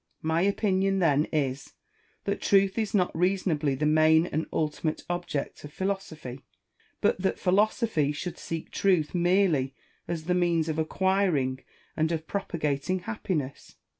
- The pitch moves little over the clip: No, average, 3.9 semitones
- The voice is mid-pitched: Yes, medium, 170 Hz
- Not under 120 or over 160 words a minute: Yes, average, 140 wpm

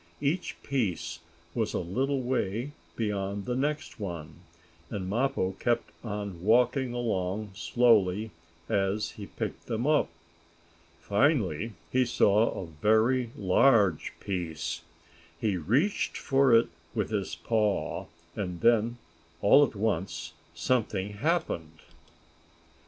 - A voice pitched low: Yes, low, 105 Hz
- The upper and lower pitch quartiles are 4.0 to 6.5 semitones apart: Yes, average, 4.6 semitones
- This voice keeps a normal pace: No, slow, 115 wpm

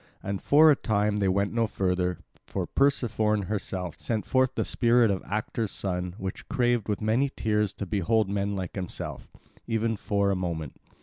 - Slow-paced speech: No, average, 175 wpm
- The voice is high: No, low, 105 Hz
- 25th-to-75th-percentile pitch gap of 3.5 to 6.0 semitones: No, average, 3.1 semitones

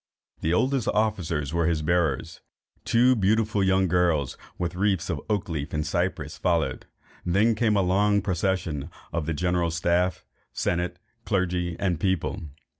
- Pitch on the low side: Yes, very low, 90 Hz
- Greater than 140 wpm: Yes, average, 150 wpm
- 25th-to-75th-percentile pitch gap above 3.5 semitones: No, average, 3.2 semitones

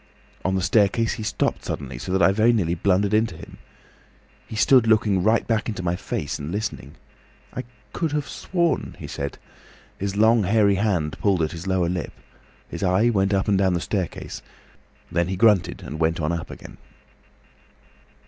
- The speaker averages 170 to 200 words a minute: Yes, average, 180 wpm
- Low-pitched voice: Yes, very low, 95 Hz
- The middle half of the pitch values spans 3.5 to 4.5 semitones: Yes, average, 4.0 semitones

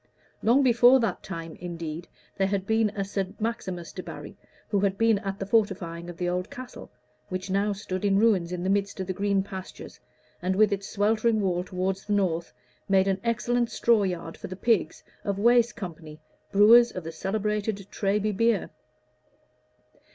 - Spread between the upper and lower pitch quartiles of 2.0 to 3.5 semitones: Yes, average, 2.8 semitones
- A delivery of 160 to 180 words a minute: Yes, average, 175 wpm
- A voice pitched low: No, high, 195 Hz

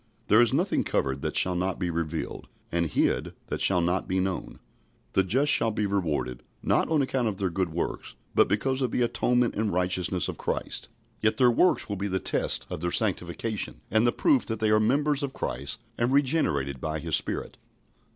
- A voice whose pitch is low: Yes, low, 100 Hz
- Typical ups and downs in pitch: No, wide, 5.7 semitones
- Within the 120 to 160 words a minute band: No, average, 200 wpm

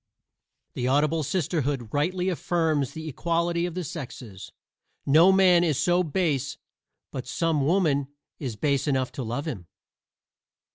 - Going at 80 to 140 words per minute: Yes, slow, 135 wpm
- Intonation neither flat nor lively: Yes, average, 4.1 semitones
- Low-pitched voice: No, medium, 155 Hz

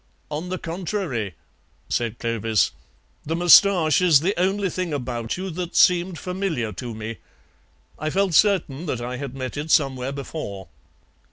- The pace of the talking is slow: No, average, 150 wpm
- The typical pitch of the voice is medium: Yes, medium, 155 Hz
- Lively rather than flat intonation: Yes, wide, 6.8 semitones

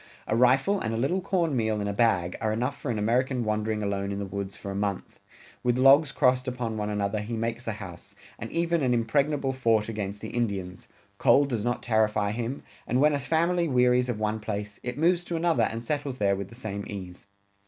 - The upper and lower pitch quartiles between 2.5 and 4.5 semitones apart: Yes, average, 4.2 semitones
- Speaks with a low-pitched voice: Yes, low, 115 Hz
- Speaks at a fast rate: Yes, fast, 220 wpm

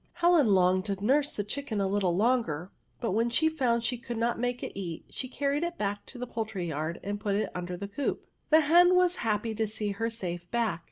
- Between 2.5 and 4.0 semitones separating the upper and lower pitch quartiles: No, average, 4.6 semitones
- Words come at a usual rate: No, fast, 240 wpm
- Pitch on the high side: Yes, high, 220 Hz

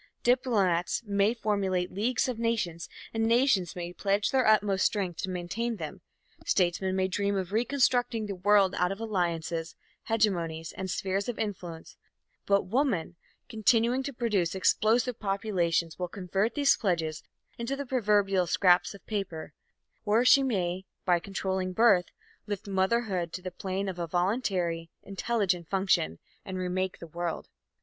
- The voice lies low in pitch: No, high, 195 Hz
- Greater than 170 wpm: No, average, 145 wpm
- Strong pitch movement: No, average, 3.9 semitones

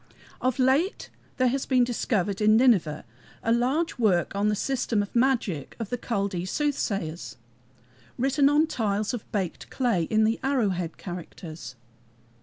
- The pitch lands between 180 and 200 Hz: No, high, 220 Hz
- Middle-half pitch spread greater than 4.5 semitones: Yes, average, 5.2 semitones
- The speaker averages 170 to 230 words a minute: No, average, 150 wpm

